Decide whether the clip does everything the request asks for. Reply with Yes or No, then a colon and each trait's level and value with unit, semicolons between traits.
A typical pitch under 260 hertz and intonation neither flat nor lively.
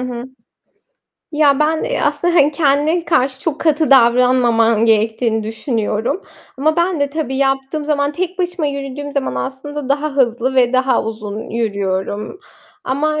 No: very high, 270 Hz; average, 4.4 semitones